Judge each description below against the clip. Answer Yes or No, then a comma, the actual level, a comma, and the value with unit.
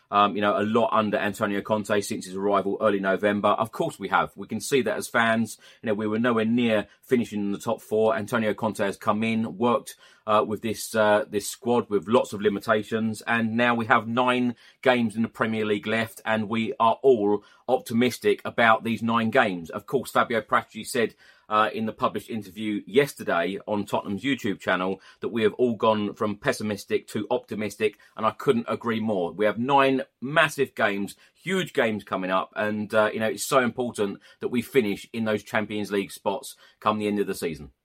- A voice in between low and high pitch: No, low, 110 Hz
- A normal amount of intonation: No, narrow, 2.1 semitones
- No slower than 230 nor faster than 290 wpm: No, fast, 205 wpm